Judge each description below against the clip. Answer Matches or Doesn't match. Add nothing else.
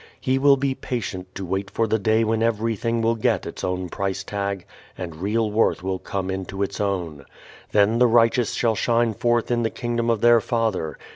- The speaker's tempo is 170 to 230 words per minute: Matches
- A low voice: Matches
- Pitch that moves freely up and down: Doesn't match